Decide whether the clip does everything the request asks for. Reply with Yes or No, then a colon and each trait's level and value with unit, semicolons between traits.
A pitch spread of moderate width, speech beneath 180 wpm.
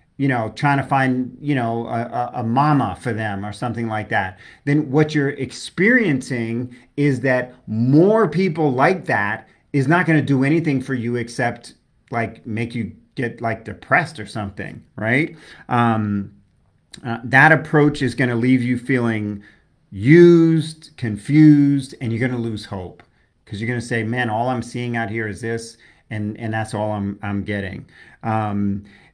Yes: average, 4.1 semitones; average, 170 wpm